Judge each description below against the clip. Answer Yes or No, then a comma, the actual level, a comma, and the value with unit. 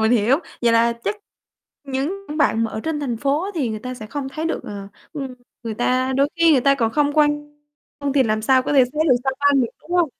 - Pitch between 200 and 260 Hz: No, very high, 270 Hz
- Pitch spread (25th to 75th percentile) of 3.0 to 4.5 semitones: Yes, average, 3.9 semitones